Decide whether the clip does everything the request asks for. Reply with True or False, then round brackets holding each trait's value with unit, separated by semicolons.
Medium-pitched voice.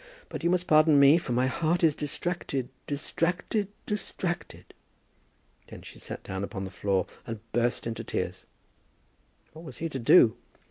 True (145 Hz)